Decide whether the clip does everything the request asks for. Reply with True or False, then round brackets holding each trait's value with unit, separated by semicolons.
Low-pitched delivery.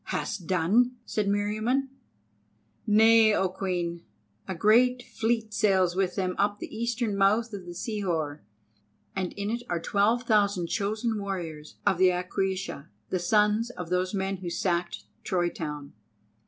False (195 Hz)